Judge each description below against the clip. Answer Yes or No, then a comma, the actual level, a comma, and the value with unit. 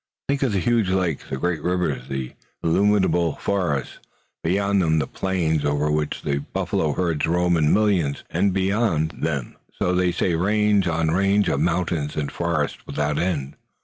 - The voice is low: Yes, very low, 85 Hz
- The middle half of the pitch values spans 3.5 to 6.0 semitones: Yes, average, 4.1 semitones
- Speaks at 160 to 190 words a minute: Yes, average, 165 wpm